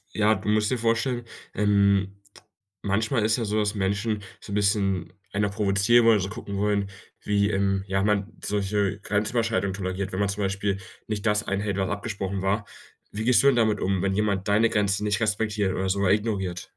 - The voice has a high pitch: No, low, 100 Hz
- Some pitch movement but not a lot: No, narrow, 1.5 semitones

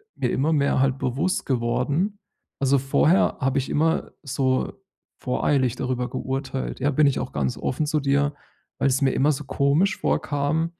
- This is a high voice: No, medium, 140 Hz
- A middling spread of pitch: No, narrow, 2.3 semitones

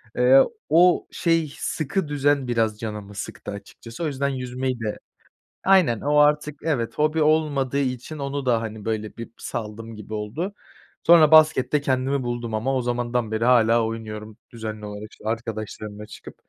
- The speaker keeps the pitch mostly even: No, average, 4.8 semitones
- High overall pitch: No, low, 125 Hz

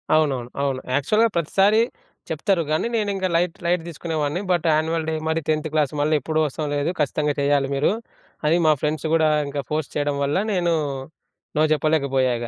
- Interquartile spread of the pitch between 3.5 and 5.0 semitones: No, average, 2.7 semitones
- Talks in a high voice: No, medium, 155 Hz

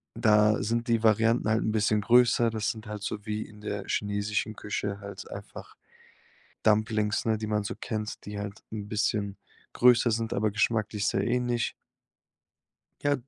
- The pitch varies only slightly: Yes, narrow, 1.5 semitones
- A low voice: Yes, low, 110 Hz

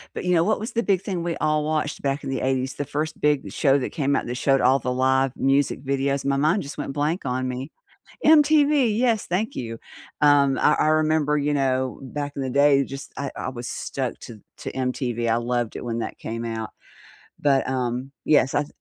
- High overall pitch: No, medium, 140 Hz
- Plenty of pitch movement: No, average, 2.8 semitones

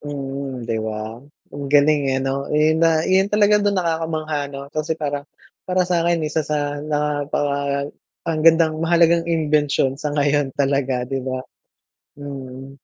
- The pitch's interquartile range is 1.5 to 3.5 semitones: Yes, average, 2.8 semitones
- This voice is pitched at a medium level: Yes, medium, 145 Hz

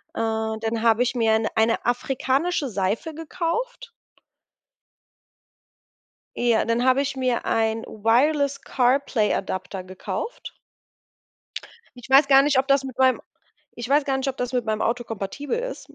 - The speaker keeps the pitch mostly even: No, average, 3.7 semitones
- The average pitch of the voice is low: No, very high, 250 Hz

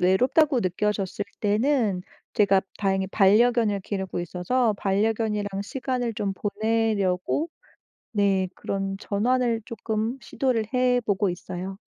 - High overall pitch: Yes, high, 210 Hz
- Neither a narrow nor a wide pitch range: Yes, average, 3.3 semitones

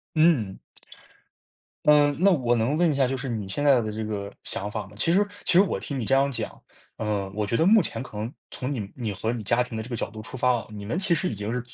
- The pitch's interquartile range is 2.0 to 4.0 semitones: No, average, 5.3 semitones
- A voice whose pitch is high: No, low, 120 Hz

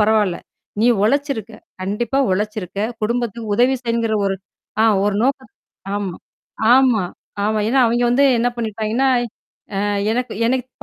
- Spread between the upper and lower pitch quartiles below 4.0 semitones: Yes, average, 2.8 semitones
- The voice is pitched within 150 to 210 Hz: No, high, 225 Hz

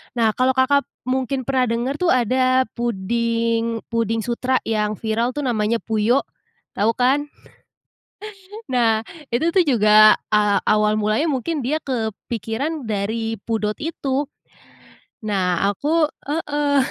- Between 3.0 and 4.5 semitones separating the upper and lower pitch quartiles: Yes, average, 3.3 semitones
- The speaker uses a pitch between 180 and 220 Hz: No, high, 235 Hz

